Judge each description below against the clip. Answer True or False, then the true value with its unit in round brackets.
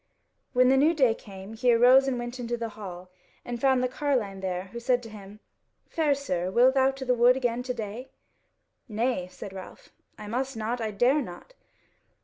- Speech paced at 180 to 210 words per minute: True (195 wpm)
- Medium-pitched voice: False (240 Hz)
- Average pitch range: True (3.8 semitones)